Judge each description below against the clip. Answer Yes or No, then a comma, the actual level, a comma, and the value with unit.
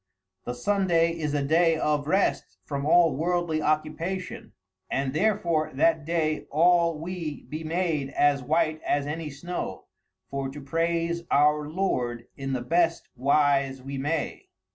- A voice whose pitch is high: No, medium, 155 Hz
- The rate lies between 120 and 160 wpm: Yes, average, 140 wpm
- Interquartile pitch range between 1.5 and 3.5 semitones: Yes, average, 3.1 semitones